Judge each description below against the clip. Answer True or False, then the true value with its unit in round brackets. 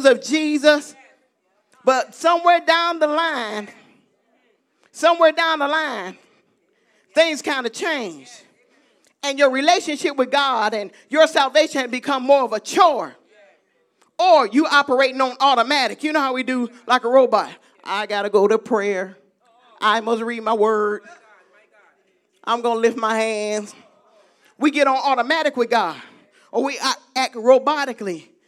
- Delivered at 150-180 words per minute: False (140 wpm)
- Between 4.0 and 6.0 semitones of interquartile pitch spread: True (5.1 semitones)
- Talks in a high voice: True (260 Hz)